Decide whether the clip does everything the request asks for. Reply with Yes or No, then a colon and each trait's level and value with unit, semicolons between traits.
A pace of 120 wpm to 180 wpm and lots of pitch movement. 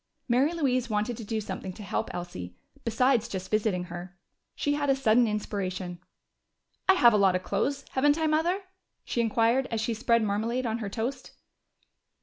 No: average, 175 wpm; average, 4.4 semitones